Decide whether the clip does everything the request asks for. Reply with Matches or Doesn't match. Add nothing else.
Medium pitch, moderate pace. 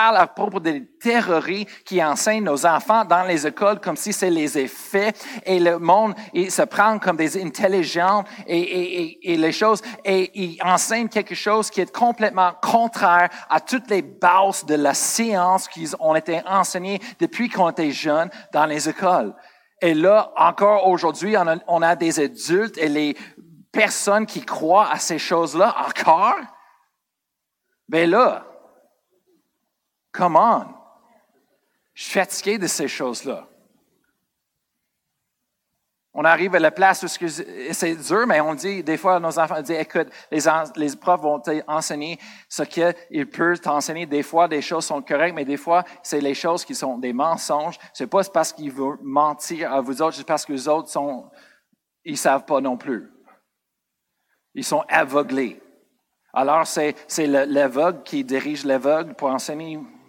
Matches